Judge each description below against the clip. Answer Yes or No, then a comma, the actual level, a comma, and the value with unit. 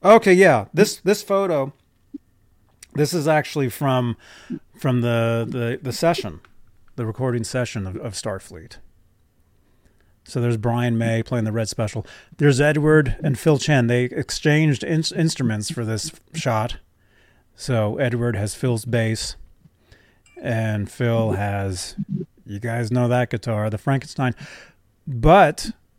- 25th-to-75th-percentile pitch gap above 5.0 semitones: Yes, wide, 5.4 semitones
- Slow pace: Yes, slow, 130 wpm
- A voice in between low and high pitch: No, low, 120 Hz